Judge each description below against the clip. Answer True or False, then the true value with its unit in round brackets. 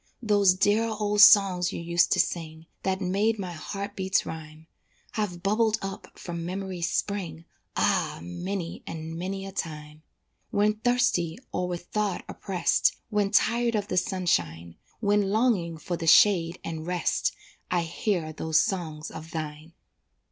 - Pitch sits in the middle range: True (180 Hz)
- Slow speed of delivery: False (150 wpm)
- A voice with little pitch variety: False (3.8 semitones)